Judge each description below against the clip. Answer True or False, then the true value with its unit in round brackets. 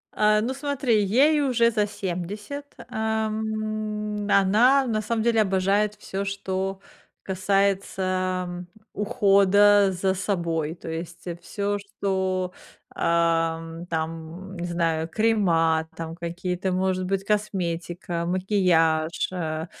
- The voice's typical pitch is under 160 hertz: False (190 Hz)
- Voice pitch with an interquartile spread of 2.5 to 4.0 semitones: True (3.6 semitones)